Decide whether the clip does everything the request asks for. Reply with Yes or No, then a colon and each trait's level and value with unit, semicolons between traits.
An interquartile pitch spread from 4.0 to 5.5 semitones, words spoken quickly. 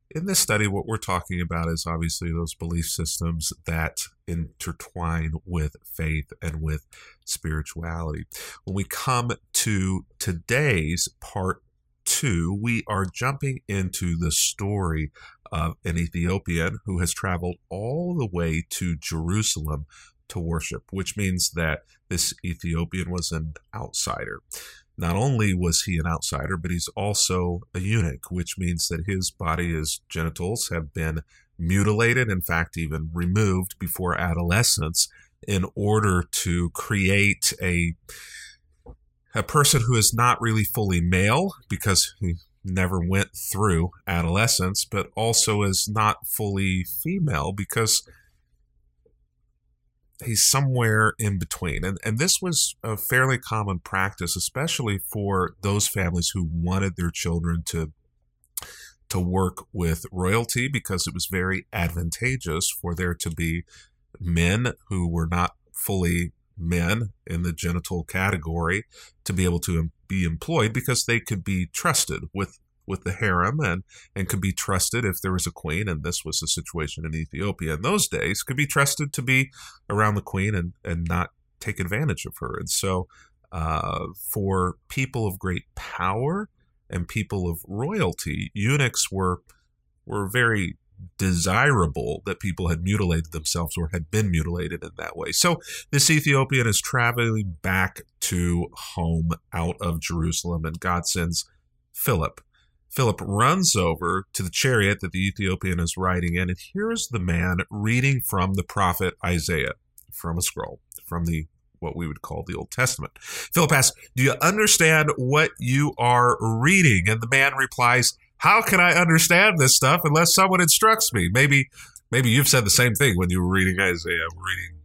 No: average, 4.6 semitones; average, 150 wpm